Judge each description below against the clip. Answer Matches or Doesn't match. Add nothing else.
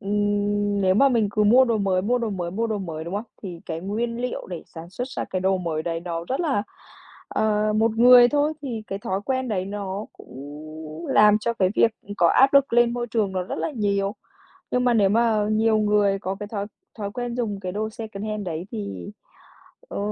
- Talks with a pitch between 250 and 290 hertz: Doesn't match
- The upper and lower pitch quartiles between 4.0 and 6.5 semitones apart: Doesn't match